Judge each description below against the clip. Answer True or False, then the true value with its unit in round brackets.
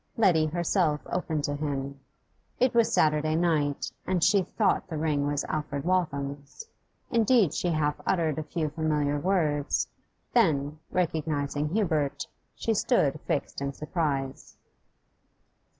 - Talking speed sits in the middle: False (125 wpm)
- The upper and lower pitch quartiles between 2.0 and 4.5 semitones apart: True (3.4 semitones)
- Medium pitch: True (155 Hz)